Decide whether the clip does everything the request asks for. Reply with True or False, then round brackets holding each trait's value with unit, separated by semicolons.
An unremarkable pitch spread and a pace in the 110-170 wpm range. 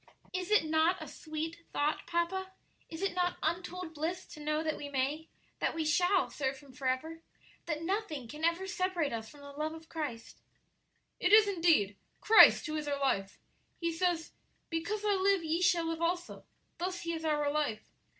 False (3.3 semitones; 185 wpm)